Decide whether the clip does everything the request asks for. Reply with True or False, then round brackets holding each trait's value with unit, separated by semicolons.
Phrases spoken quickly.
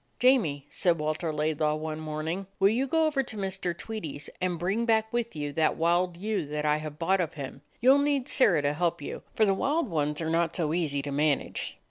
True (225 wpm)